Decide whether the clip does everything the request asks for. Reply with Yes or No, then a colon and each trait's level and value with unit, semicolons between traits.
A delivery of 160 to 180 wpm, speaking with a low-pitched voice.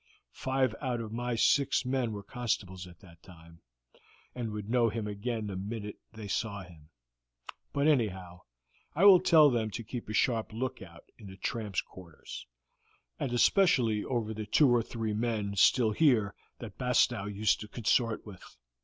Yes: average, 165 wpm; low, 110 Hz